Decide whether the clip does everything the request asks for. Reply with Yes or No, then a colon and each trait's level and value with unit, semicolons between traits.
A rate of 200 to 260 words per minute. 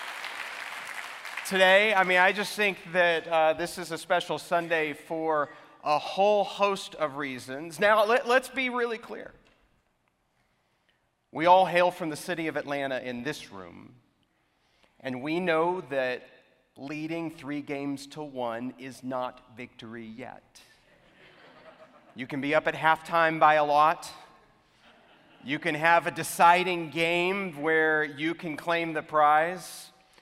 No: average, 140 wpm